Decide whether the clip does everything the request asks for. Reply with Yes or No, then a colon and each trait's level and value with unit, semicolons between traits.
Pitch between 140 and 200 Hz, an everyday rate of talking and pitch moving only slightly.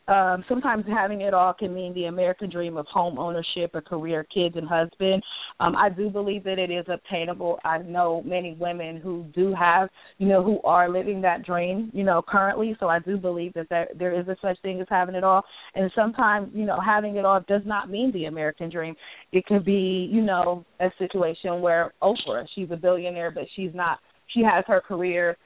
No: medium, 185 Hz; fast, 210 wpm; narrow, 2.3 semitones